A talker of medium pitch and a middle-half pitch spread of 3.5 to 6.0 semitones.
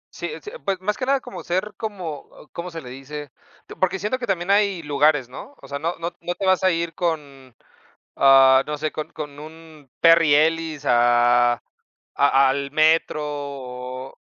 Yes: medium, 155 Hz; average, 4.3 semitones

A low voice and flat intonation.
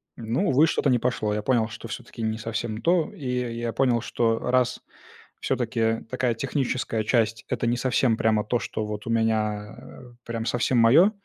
Yes: low, 115 Hz; narrow, 2.1 semitones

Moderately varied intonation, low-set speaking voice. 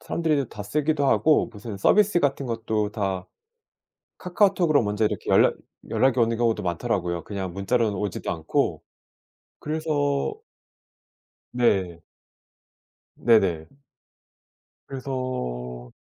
No: wide, 6.2 semitones; low, 115 Hz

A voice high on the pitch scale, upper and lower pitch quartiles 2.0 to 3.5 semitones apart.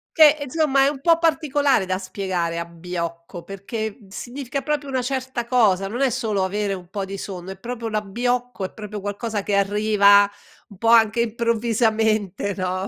No: high, 215 Hz; average, 4.3 semitones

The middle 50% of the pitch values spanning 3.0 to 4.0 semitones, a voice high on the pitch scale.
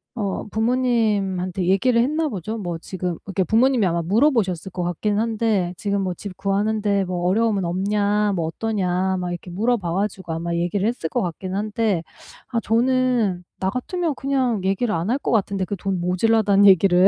Yes: average, 3.7 semitones; high, 200 Hz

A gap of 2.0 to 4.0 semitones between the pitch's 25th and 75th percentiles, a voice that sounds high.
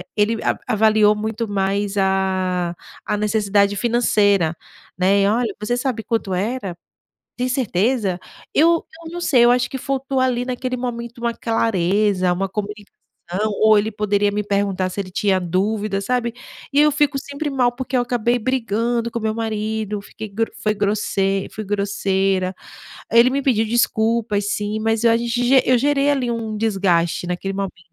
Yes: average, 3.4 semitones; high, 215 Hz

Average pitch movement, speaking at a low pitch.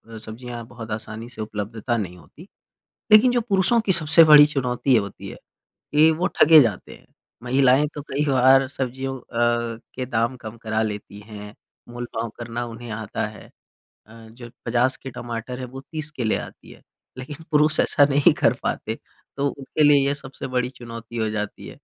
Yes: average, 3.7 semitones; low, 125 Hz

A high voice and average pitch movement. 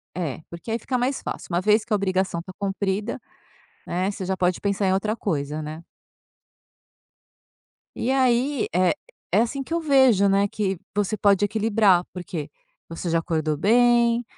Yes: high, 200 Hz; average, 4.4 semitones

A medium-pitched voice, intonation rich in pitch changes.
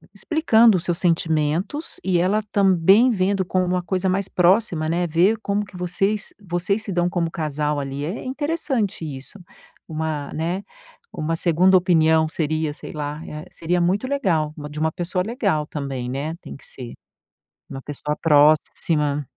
No: medium, 170 Hz; average, 4.1 semitones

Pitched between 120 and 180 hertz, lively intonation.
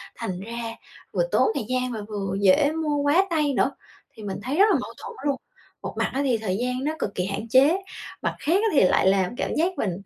No: very high, 250 Hz; wide, 6.5 semitones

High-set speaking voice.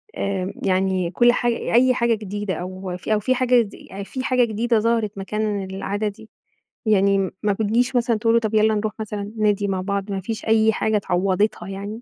Yes: high, 210 Hz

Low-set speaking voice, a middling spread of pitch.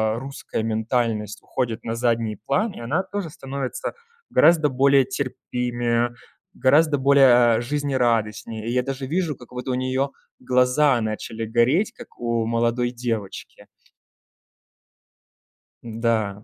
Yes: low, 125 Hz; average, 3.0 semitones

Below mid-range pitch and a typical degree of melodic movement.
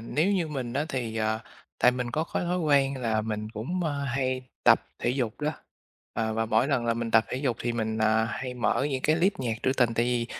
Yes: low, 125 Hz; average, 3.5 semitones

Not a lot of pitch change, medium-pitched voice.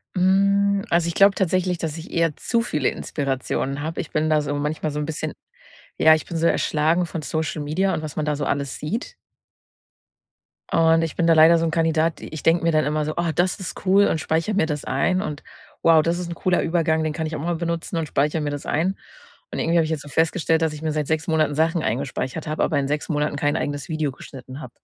Yes: narrow, 2.1 semitones; medium, 160 Hz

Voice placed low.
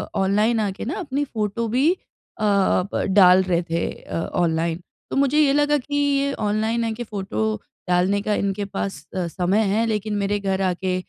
No: high, 205 Hz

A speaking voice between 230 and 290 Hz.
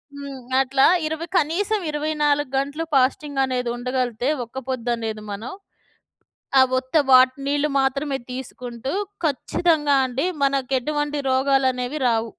Yes: very high, 270 Hz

